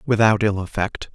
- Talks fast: No, average, 155 wpm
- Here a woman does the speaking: No, male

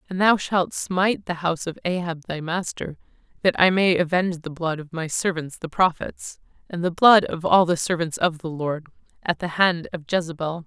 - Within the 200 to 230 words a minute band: Yes, fast, 205 wpm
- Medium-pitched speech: Yes, medium, 170 Hz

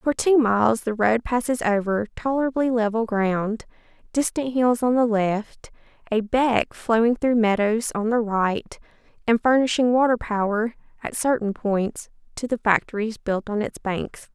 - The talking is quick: No, average, 155 wpm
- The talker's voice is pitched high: Yes, high, 225 Hz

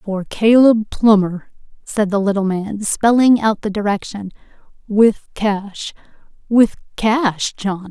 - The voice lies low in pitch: No, high, 210 Hz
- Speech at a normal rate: No, slow, 120 wpm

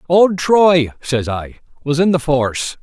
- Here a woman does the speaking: No, male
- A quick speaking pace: No, average, 170 wpm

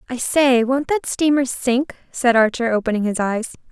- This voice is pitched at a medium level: No, very high, 250 Hz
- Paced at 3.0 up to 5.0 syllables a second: Yes, 4.8 syllables/s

